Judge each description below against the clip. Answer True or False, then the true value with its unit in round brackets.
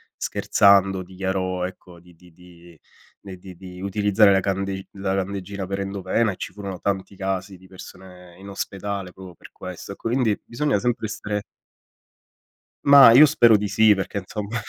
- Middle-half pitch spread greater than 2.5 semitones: False (1.8 semitones)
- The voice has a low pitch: True (95 Hz)